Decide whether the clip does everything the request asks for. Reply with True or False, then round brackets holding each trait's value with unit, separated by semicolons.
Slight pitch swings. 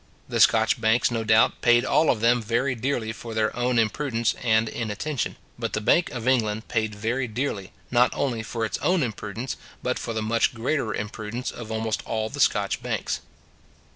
True (2.1 semitones)